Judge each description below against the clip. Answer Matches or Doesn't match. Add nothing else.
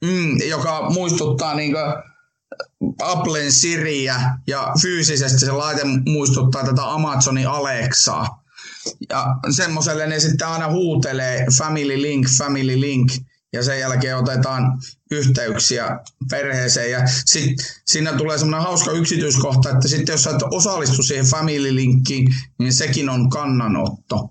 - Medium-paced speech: Matches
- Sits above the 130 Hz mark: Matches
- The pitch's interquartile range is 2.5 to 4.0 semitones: Matches